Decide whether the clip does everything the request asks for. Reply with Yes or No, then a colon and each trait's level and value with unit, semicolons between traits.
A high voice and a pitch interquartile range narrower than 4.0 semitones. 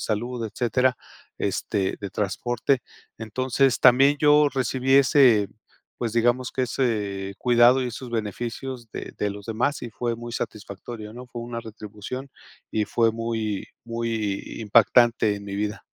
No: low, 115 Hz; average, 2.9 semitones